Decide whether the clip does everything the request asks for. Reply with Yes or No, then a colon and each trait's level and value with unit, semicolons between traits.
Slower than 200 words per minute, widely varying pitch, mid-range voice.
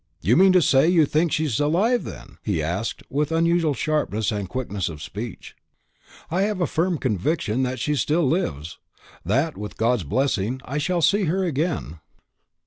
Yes: average, 170 wpm; wide, 7.7 semitones; medium, 145 Hz